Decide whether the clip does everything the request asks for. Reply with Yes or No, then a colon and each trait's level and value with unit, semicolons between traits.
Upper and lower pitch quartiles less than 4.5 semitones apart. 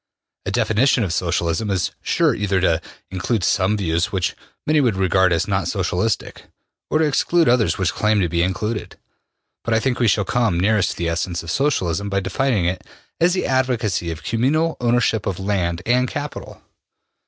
No: average, 5.2 semitones